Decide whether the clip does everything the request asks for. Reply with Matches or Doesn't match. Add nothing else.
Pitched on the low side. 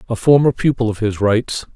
Matches